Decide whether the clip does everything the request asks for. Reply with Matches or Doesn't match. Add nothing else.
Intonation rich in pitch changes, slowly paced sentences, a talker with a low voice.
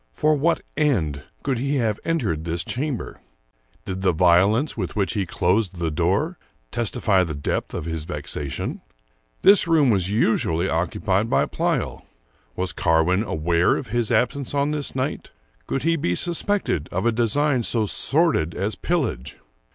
Doesn't match